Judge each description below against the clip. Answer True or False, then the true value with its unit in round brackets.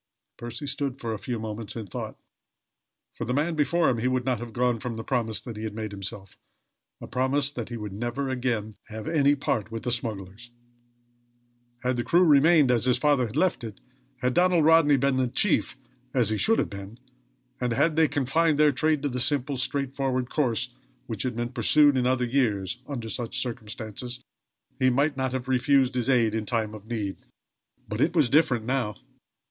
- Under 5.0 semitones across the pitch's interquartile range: True (3.7 semitones)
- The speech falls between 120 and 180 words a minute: False (195 wpm)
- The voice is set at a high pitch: False (125 Hz)